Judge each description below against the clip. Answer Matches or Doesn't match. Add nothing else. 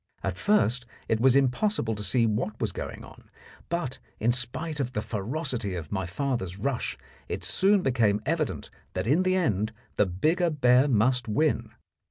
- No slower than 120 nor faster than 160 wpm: Doesn't match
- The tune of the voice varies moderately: Doesn't match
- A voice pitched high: Doesn't match